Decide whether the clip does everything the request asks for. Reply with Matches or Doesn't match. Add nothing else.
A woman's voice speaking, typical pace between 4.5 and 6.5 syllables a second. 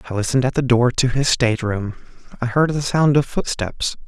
Doesn't match